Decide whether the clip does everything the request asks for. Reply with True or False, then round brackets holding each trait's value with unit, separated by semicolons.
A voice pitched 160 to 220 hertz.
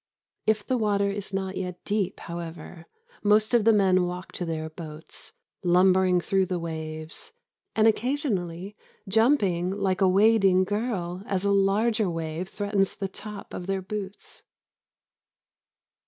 True (190 Hz)